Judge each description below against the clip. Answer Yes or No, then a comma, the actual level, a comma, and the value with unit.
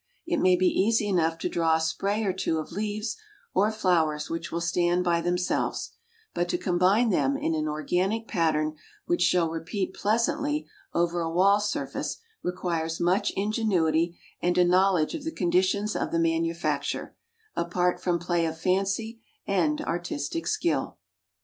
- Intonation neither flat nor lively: Yes, average, 3.3 semitones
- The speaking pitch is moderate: Yes, medium, 175 Hz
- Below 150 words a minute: No, average, 155 wpm